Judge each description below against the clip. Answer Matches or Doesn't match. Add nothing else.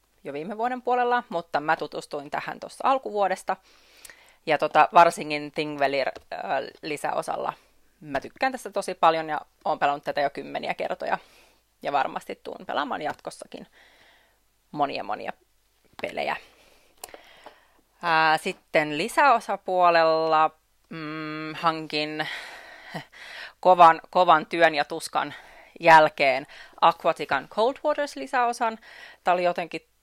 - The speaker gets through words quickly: Doesn't match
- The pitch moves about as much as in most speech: Doesn't match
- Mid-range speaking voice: Matches